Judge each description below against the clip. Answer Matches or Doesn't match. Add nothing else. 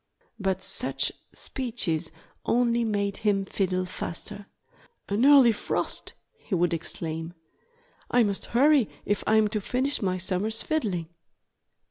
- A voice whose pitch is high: Matches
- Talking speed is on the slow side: Matches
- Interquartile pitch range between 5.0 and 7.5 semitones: Doesn't match